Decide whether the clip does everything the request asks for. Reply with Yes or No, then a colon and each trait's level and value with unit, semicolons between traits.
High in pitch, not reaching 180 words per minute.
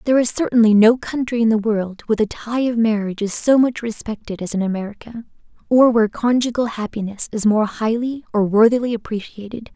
No: high, 225 Hz; average, 185 wpm